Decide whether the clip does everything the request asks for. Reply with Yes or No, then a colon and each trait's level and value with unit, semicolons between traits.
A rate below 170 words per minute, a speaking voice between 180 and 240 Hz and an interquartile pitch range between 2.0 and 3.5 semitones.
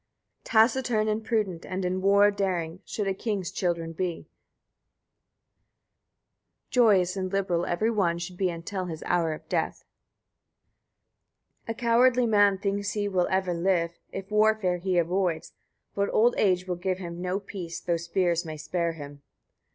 Yes: average, 155 wpm; medium, 185 Hz; average, 2.9 semitones